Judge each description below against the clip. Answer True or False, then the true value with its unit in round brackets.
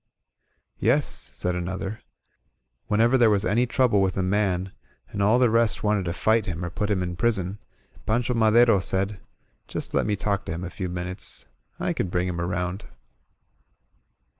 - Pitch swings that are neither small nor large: True (3.3 semitones)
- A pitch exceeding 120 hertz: False (100 Hz)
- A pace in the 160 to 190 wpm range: True (175 wpm)